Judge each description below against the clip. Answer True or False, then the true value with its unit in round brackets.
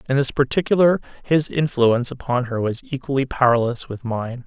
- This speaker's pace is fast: False (160 wpm)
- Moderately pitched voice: False (130 Hz)